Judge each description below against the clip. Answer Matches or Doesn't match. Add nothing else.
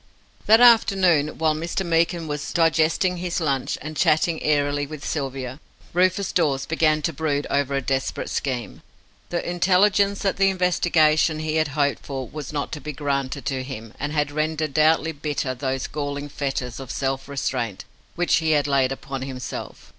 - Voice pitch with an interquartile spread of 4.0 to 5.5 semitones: Doesn't match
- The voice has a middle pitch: Matches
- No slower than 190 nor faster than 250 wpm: Doesn't match